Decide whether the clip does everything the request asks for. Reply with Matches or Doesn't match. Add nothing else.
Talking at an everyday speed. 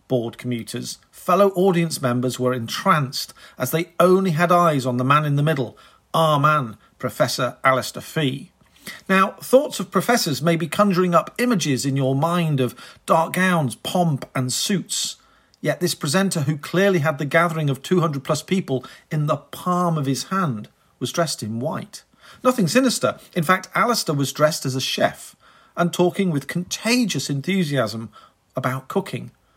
Matches